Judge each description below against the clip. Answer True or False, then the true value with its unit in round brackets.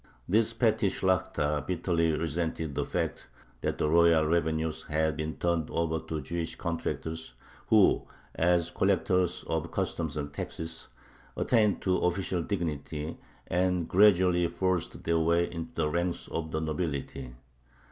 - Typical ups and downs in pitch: False (2.3 semitones)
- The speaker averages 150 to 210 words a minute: False (135 wpm)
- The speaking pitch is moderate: False (85 Hz)